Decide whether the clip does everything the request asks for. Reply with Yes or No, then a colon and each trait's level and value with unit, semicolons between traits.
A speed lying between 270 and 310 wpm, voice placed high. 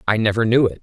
No: fast, 290 wpm; low, 110 Hz